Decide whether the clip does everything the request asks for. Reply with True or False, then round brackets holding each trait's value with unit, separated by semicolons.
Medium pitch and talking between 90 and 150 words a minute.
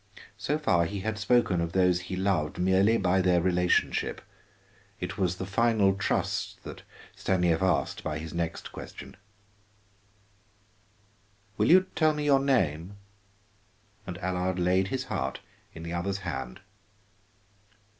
False (95 Hz; 135 wpm)